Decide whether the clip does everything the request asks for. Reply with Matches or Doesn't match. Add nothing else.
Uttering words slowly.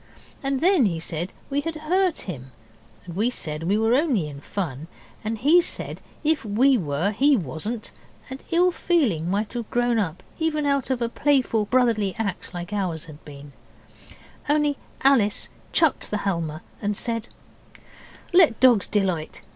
Doesn't match